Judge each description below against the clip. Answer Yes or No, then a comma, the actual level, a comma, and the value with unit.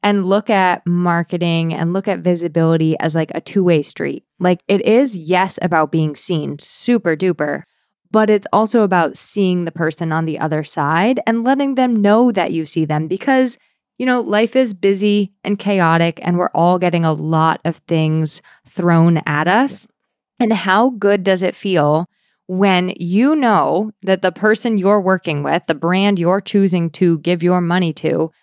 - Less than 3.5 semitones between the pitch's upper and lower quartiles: No, average, 3.8 semitones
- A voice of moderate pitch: Yes, medium, 180 Hz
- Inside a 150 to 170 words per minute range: No, average, 180 wpm